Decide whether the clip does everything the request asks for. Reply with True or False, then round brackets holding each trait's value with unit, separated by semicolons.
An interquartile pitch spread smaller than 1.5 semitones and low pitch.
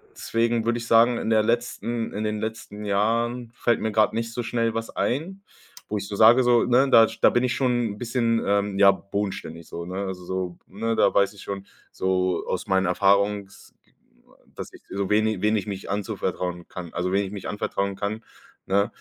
False (2.8 semitones; 105 Hz)